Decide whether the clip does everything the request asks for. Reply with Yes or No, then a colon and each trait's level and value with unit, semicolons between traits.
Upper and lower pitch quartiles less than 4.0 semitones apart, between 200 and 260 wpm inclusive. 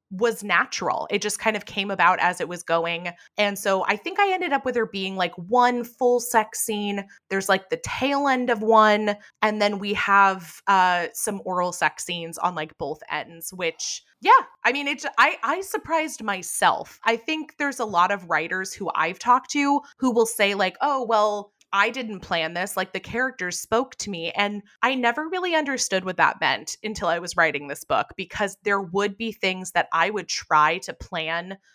No: average, 4.8 semitones; fast, 205 wpm